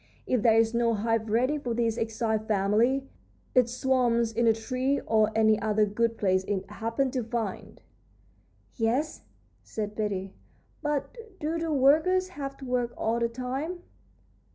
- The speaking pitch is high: Yes, high, 235 Hz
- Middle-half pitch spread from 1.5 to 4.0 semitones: Yes, average, 3.2 semitones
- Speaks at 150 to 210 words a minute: Yes, average, 155 wpm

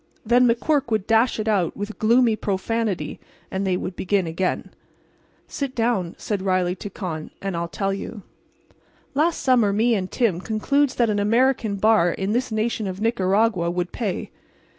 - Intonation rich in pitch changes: No, average, 3.6 semitones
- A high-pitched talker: Yes, high, 210 Hz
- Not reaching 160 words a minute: No, average, 165 wpm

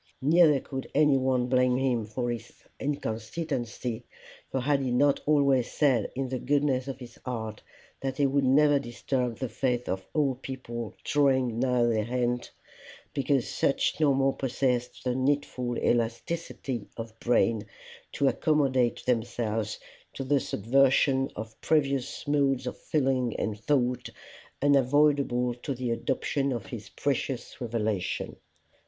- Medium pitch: No, low, 130 Hz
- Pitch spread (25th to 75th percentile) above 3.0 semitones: No, narrow, 2.6 semitones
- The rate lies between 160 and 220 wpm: No, slow, 135 wpm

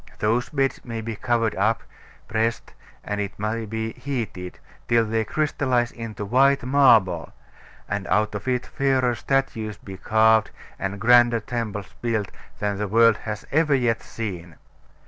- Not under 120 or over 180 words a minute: Yes, average, 145 wpm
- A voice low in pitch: Yes, low, 115 Hz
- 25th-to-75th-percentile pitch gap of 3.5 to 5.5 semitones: No, average, 2.8 semitones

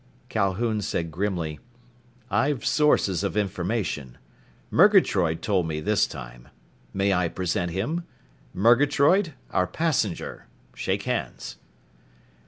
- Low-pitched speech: Yes, low, 100 Hz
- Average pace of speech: No, slow, 100 wpm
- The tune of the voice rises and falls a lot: Yes, wide, 5.7 semitones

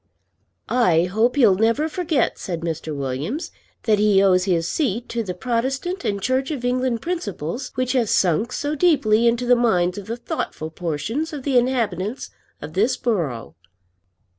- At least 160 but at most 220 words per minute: Yes, average, 165 wpm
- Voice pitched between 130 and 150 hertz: No, high, 230 Hz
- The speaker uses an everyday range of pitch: No, wide, 6.0 semitones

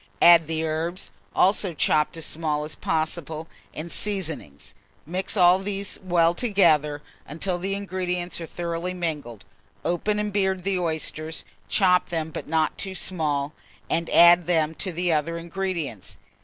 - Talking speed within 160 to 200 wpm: No, average, 145 wpm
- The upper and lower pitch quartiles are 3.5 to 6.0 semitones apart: No, average, 2.8 semitones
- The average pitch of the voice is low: No, medium, 170 Hz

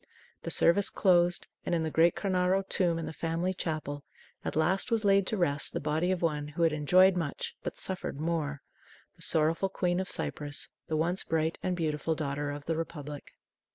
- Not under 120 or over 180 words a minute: No, average, 190 wpm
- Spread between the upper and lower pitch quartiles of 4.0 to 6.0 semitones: No, average, 3.2 semitones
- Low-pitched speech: No, medium, 165 Hz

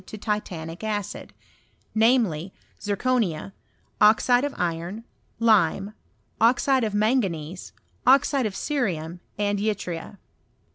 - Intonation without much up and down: No, average, 4.6 semitones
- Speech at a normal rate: No, slow, 100 wpm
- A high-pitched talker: Yes, high, 210 Hz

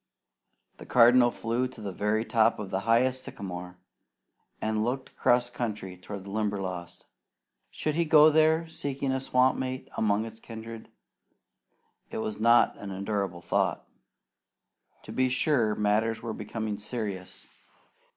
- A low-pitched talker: Yes, low, 110 Hz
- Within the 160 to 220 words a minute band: No, average, 140 wpm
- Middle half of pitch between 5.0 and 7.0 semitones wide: No, average, 3.7 semitones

